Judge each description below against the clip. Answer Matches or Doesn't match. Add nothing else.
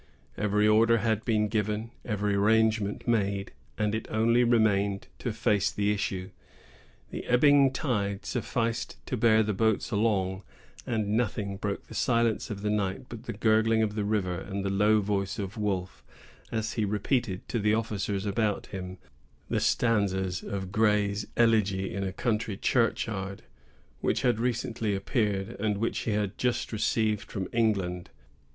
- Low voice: Matches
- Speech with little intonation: Matches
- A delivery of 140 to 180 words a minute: Matches